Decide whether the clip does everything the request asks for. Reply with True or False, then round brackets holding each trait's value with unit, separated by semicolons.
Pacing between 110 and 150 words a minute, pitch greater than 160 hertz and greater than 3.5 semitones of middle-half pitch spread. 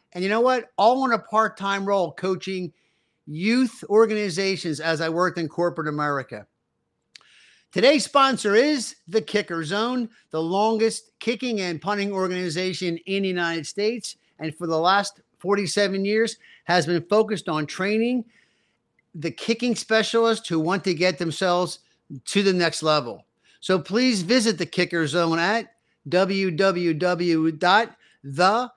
True (140 wpm; 190 Hz; 4.4 semitones)